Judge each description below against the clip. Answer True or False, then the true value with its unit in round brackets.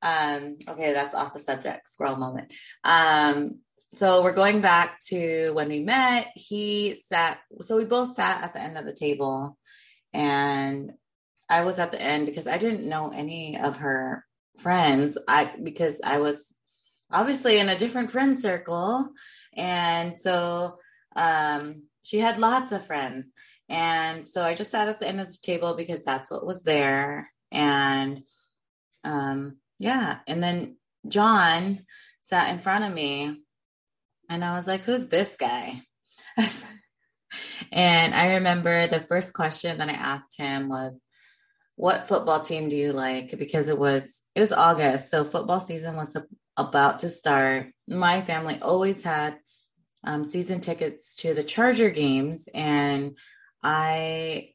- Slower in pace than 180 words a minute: True (150 wpm)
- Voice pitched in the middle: True (165 Hz)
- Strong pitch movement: False (4.7 semitones)